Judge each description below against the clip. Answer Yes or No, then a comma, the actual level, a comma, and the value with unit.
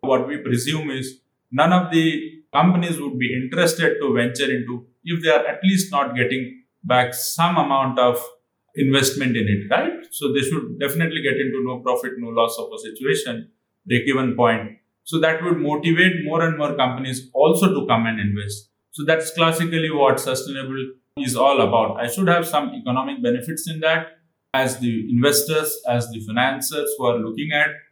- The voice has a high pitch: No, low, 135 Hz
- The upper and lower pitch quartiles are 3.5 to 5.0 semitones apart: Yes, average, 4.3 semitones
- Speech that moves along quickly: No, average, 180 wpm